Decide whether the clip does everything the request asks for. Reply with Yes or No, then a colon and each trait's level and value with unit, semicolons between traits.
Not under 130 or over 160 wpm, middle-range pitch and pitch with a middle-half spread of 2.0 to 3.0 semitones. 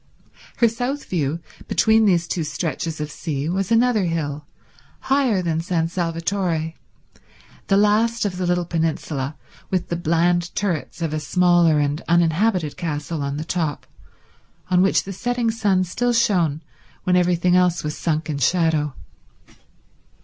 No: average, 145 wpm; medium, 175 Hz; average, 3.4 semitones